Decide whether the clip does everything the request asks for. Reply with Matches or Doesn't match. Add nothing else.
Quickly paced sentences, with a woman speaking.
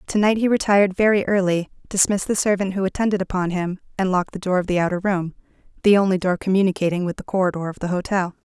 Matches